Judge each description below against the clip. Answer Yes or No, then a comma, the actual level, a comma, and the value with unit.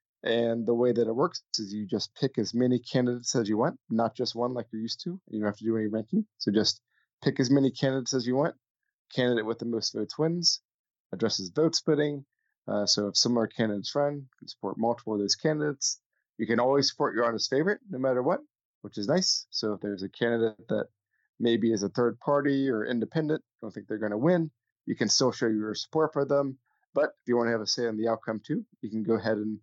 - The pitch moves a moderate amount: Yes, average, 4.1 semitones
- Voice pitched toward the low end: Yes, low, 120 Hz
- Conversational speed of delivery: No, fast, 240 wpm